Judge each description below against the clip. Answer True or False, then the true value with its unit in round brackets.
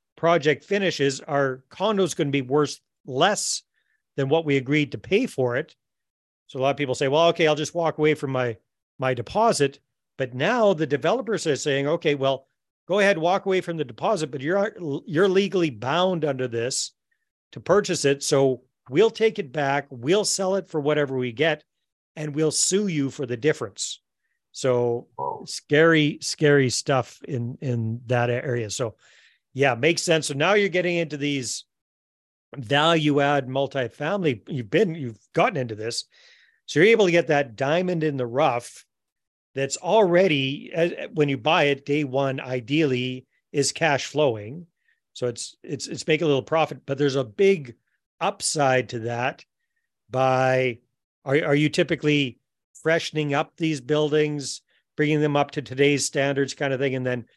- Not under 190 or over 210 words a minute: False (170 wpm)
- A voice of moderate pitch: True (145 Hz)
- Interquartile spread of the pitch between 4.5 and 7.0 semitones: False (3.8 semitones)